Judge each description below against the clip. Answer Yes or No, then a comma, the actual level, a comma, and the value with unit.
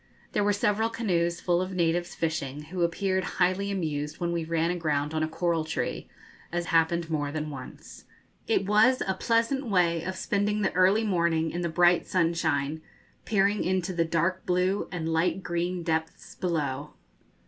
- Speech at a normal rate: Yes, average, 170 wpm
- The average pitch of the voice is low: No, medium, 175 Hz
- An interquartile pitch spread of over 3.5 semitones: No, narrow, 2.6 semitones